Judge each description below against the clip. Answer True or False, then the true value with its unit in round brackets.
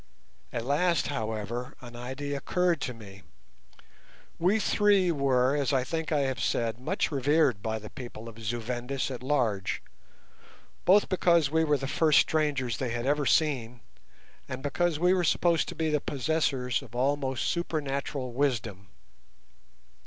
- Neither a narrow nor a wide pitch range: True (4.4 semitones)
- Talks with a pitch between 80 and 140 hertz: True (135 Hz)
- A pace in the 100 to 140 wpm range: False (150 wpm)